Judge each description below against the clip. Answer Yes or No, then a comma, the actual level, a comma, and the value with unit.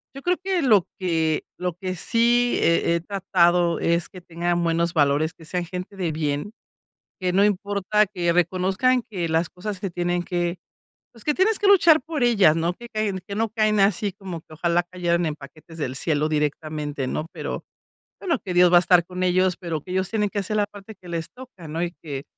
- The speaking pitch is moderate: Yes, medium, 180 Hz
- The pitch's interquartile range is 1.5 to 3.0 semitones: No, average, 3.6 semitones